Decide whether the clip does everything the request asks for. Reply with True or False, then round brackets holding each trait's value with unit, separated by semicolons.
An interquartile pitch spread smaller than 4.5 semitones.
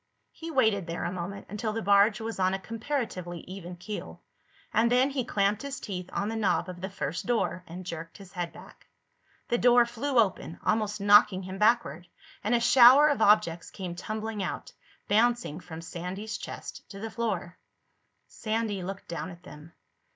True (3.9 semitones)